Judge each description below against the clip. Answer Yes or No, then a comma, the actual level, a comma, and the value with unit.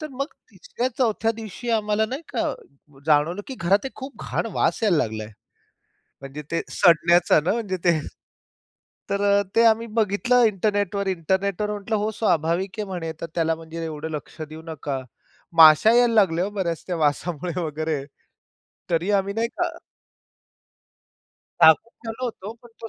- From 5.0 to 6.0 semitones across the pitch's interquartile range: Yes, average, 5.3 semitones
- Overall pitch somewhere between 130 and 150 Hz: No, high, 190 Hz